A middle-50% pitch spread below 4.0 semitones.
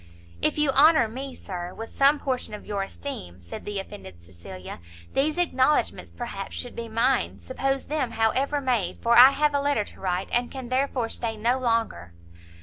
No: average, 5.1 semitones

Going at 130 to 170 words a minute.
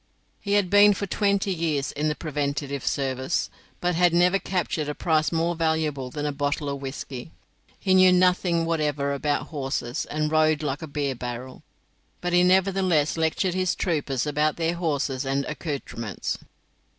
Yes: average, 165 wpm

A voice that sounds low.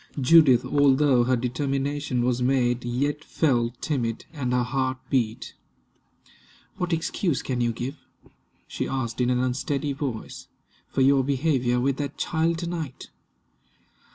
Yes: low, 130 Hz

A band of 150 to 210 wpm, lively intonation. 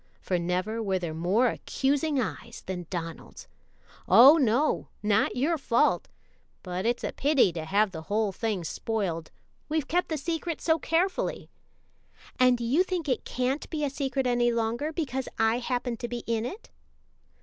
Yes: average, 165 wpm; wide, 5.9 semitones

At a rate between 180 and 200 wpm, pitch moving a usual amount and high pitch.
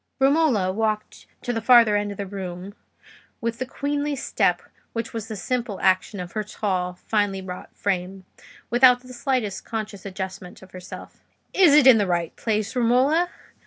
No: average, 165 wpm; average, 4.7 semitones; high, 215 Hz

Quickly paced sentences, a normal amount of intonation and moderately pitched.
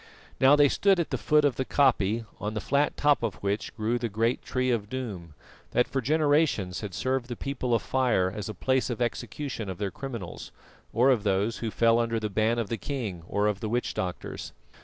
No: fast, 220 wpm; average, 4.0 semitones; low, 115 Hz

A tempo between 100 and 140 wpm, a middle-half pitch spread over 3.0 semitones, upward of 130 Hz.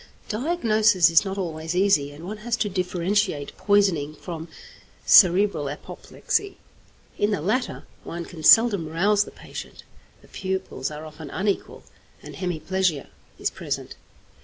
Yes: slow, 135 wpm; average, 4.3 semitones; medium, 185 Hz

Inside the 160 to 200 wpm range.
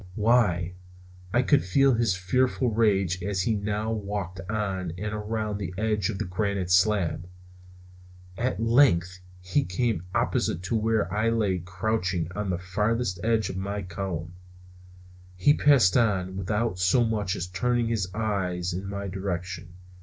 No: average, 150 wpm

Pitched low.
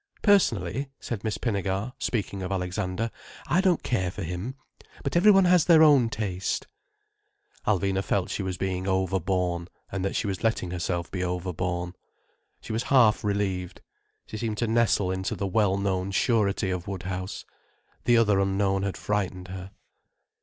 Yes: very low, 95 Hz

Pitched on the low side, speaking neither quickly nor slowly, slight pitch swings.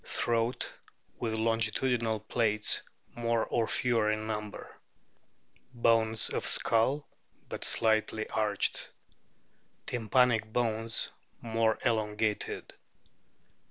No: low, 110 Hz; slow, 85 wpm; narrow, 1.3 semitones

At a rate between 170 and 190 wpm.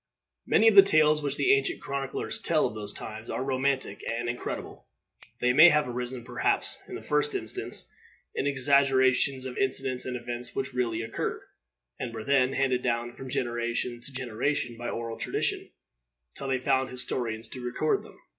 Yes: average, 175 wpm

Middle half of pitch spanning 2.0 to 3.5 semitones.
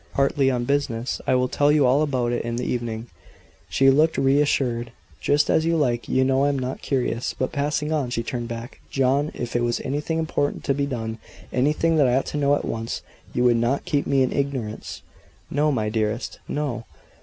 Yes: average, 3.2 semitones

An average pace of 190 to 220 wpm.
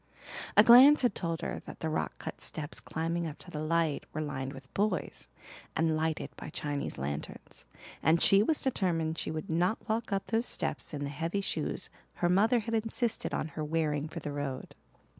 Yes: average, 195 wpm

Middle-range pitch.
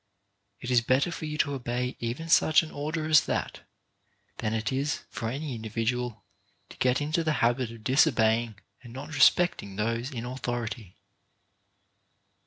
No: low, 125 Hz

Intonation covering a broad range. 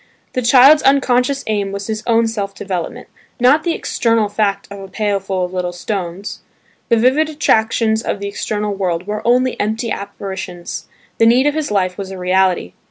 No: average, 3.8 semitones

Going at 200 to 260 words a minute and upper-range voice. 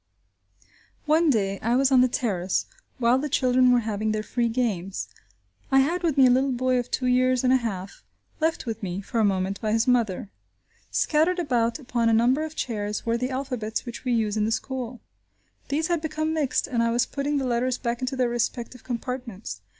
Yes: fast, 205 wpm; high, 245 Hz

